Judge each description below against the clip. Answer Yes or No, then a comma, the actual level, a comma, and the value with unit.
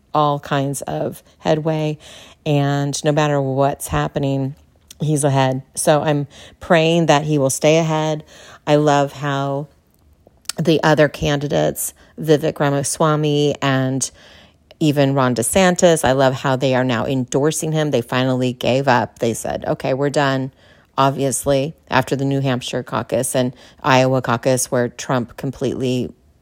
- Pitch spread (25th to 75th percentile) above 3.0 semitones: No, narrow, 2.6 semitones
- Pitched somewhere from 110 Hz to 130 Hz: No, medium, 140 Hz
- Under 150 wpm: Yes, slow, 135 wpm